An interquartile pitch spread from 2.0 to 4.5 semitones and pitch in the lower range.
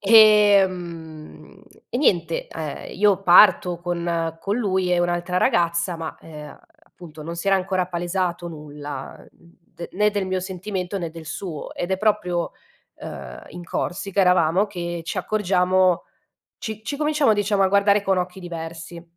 No: average, 2.7 semitones; medium, 180 Hz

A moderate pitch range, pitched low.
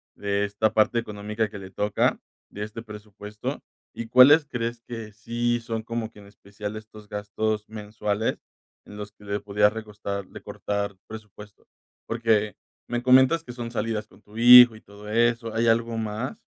No: narrow, 2.1 semitones; low, 110 Hz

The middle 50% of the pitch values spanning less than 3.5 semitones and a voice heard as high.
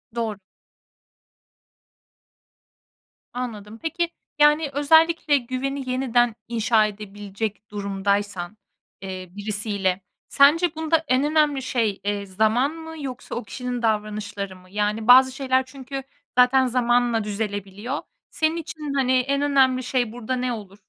No: average, 4.7 semitones; high, 245 Hz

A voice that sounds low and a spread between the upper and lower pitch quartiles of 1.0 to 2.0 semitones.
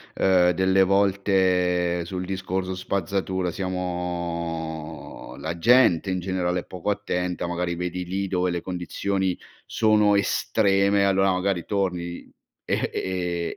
Yes: very low, 90 Hz; narrow, 1.7 semitones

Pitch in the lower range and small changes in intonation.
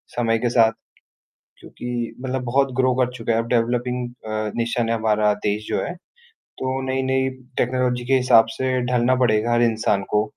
Yes: low, 120 Hz; narrow, 2.0 semitones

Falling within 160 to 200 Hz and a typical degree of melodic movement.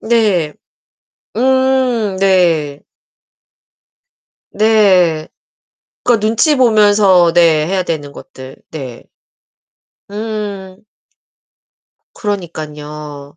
No: high, 190 Hz; wide, 5.8 semitones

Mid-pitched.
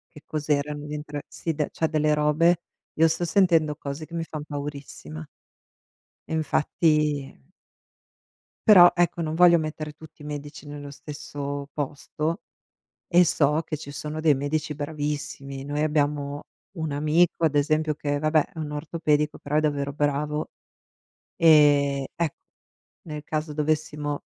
Yes: medium, 150 Hz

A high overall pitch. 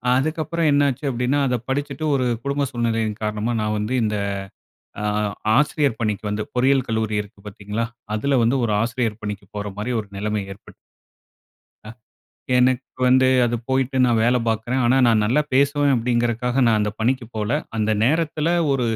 No: low, 120 Hz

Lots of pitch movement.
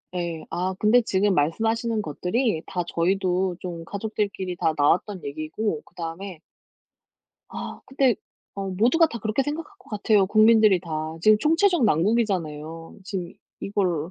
No: average, 4.4 semitones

